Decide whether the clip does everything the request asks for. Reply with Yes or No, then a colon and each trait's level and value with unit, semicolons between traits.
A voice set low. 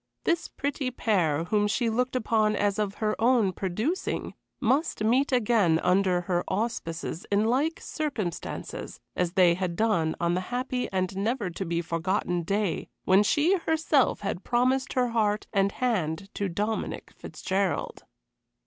No: high, 210 Hz